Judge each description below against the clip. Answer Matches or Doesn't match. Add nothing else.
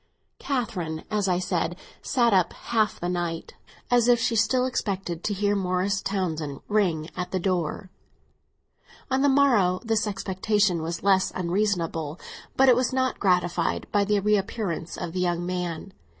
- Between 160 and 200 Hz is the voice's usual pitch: Matches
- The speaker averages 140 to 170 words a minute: Matches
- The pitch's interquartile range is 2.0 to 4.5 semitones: Matches